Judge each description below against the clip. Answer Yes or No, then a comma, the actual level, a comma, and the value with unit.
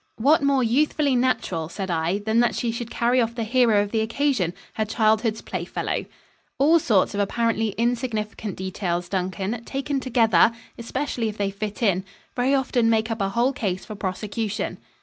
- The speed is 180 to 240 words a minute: No, average, 170 wpm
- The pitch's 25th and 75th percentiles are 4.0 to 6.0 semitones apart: No, average, 3.3 semitones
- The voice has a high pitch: Yes, high, 225 Hz